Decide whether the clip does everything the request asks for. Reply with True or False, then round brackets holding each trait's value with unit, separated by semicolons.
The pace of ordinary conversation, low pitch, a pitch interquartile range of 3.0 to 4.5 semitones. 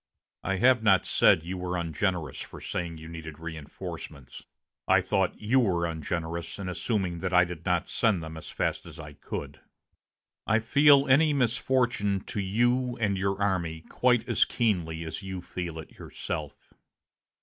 False (160 wpm; 95 Hz; 5.1 semitones)